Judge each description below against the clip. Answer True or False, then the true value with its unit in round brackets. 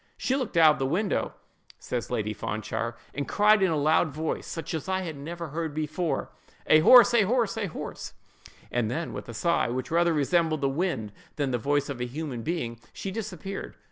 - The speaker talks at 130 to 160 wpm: False (190 wpm)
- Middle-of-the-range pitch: True (155 Hz)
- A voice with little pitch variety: False (5.0 semitones)